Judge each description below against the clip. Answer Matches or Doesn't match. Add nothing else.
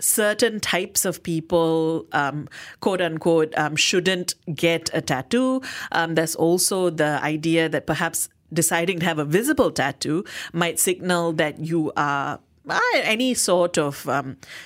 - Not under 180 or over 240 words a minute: Doesn't match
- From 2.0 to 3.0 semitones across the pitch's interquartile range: Matches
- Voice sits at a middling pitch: Matches